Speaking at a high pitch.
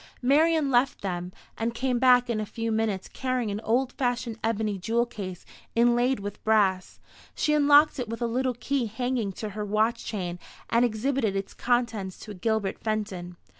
Yes: high, 230 Hz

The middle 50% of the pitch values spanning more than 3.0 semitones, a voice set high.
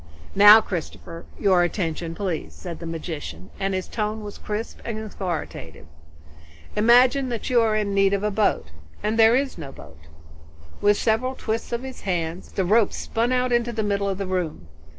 Yes: average, 4.3 semitones; high, 205 Hz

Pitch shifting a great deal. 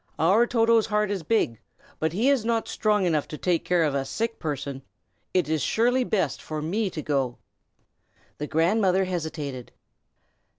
Yes: wide, 6.4 semitones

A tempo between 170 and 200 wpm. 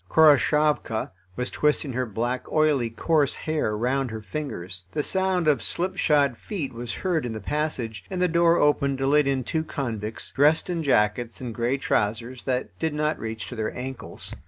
Yes: average, 180 wpm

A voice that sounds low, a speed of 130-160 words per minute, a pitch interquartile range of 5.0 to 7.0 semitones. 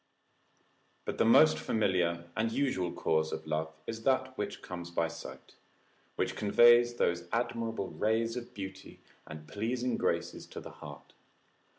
Yes: low, 105 Hz; average, 145 wpm; wide, 5.6 semitones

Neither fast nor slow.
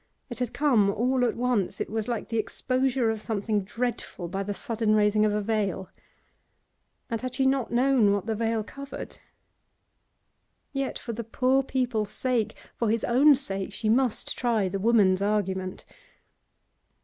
Yes: average, 160 wpm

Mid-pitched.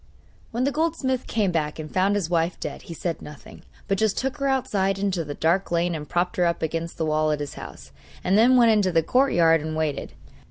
Yes: medium, 180 Hz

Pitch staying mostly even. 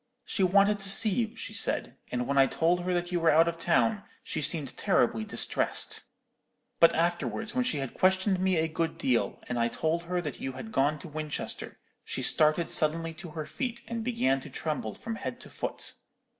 No: average, 4.0 semitones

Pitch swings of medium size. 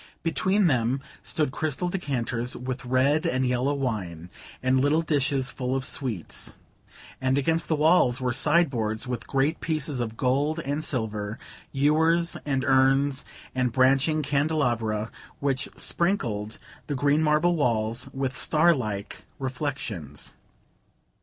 Yes: average, 3.6 semitones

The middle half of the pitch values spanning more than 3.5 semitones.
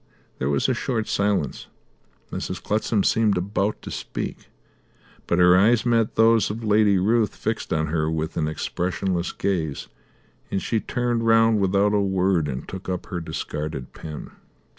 Yes: average, 4.7 semitones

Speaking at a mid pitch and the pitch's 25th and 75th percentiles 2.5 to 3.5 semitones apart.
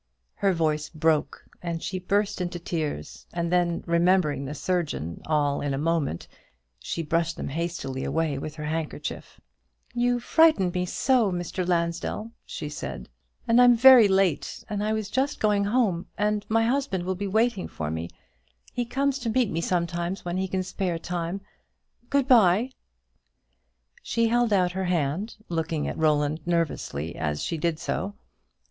No: medium, 175 Hz; average, 4.7 semitones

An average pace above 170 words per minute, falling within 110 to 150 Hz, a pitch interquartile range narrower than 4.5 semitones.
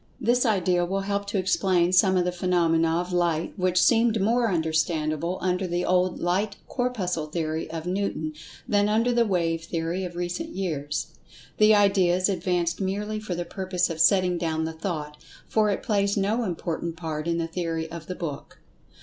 No: average, 180 wpm; medium, 180 Hz; average, 3.2 semitones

